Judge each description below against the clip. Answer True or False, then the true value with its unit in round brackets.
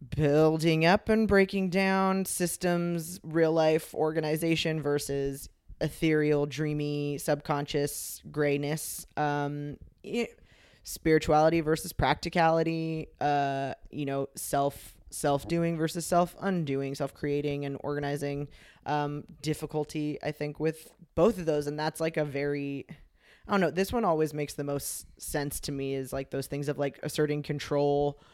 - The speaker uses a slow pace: True (130 wpm)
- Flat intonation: True (2.2 semitones)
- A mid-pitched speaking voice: True (150 Hz)